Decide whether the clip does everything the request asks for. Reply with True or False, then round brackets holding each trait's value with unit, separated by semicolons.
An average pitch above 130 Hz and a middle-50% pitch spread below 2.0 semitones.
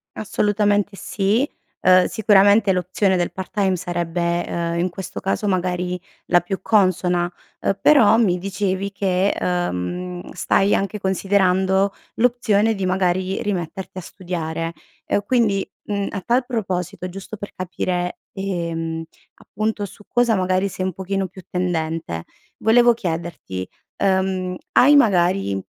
False (190 Hz; 2.3 semitones)